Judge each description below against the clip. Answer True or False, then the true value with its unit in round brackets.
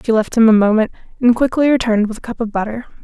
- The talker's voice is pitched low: False (230 Hz)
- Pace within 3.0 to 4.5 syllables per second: False (7.2 syllables/s)